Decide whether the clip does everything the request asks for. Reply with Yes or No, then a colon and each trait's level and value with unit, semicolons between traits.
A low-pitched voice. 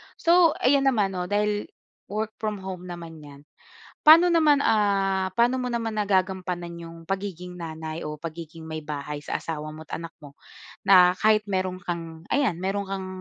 No: medium, 185 Hz